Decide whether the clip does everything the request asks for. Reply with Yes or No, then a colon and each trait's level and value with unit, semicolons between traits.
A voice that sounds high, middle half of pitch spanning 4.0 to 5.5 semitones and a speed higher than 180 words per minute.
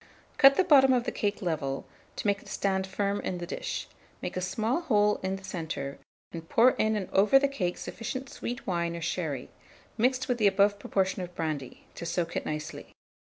Yes: high, 195 Hz; average, 5.0 semitones; fast, 205 wpm